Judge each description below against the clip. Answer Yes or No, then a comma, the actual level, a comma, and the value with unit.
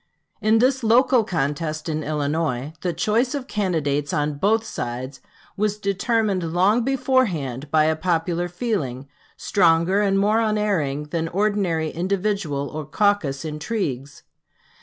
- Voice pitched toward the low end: No, medium, 175 Hz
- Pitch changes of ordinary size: No, wide, 5.9 semitones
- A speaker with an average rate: No, slow, 125 wpm